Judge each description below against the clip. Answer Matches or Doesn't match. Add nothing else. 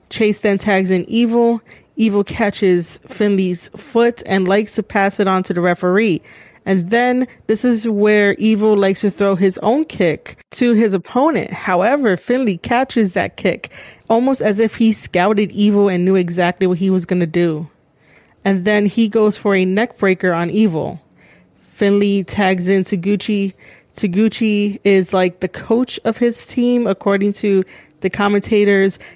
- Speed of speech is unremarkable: Matches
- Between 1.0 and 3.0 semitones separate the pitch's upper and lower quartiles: Matches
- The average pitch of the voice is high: Matches